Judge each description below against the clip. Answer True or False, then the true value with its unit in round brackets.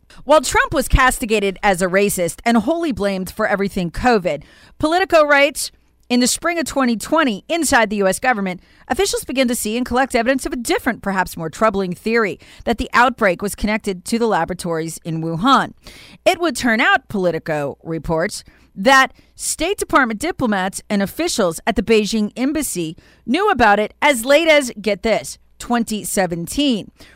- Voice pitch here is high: True (230 Hz)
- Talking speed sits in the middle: True (160 wpm)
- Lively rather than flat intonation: True (6.2 semitones)